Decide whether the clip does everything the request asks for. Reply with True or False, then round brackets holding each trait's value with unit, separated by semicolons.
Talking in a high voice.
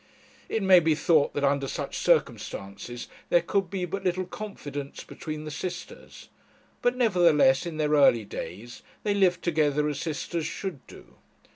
False (155 Hz)